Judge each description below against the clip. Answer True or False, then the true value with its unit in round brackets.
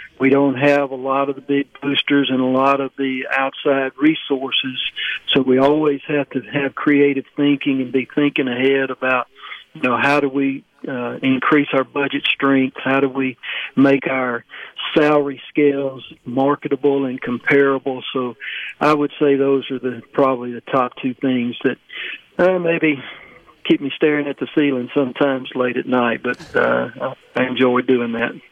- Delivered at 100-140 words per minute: False (170 wpm)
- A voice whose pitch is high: False (135 Hz)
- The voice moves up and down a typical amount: False (1.7 semitones)